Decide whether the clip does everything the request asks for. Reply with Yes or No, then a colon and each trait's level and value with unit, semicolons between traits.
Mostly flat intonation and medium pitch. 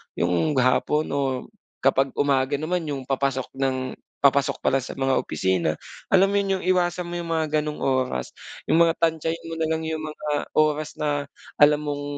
No: average, 3.2 semitones; medium, 150 Hz